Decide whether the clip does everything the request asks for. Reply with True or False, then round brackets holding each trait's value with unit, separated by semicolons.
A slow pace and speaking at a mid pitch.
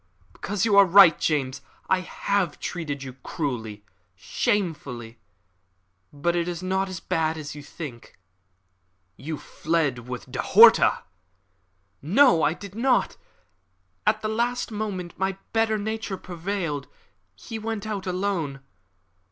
True (125 wpm; 175 Hz)